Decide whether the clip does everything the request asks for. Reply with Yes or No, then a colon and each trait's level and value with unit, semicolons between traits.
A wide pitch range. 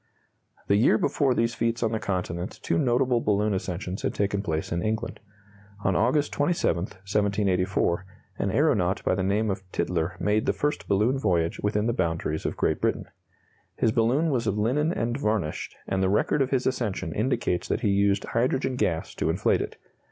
No: average, 4.2 semitones